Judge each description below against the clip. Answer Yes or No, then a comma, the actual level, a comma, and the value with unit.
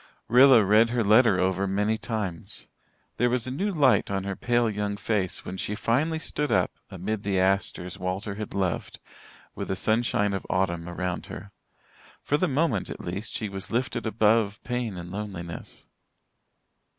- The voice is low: Yes, low, 105 Hz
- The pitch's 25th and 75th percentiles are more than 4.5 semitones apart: No, average, 3.7 semitones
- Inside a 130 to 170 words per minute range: Yes, average, 165 wpm